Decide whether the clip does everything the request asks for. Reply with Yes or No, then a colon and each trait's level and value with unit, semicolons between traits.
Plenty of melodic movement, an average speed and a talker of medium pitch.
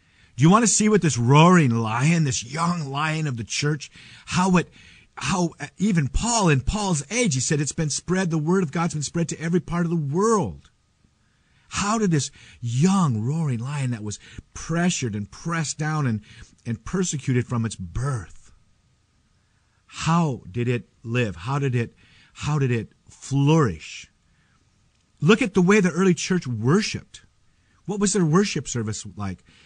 Yes: wide, 6.8 semitones; average, 170 wpm; medium, 150 Hz